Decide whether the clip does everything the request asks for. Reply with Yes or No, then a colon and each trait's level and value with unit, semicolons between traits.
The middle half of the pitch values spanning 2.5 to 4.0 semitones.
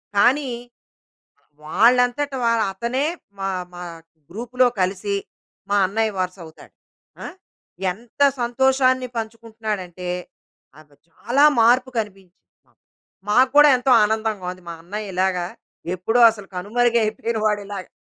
No: average, 4.4 semitones